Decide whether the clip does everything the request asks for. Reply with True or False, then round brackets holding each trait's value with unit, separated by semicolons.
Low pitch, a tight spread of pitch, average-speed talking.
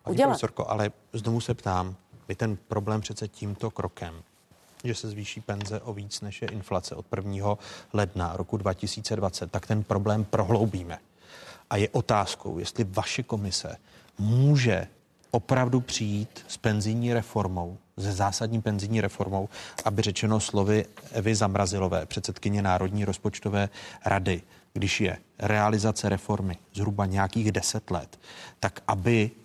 True (105 Hz; 2.3 semitones; 130 wpm)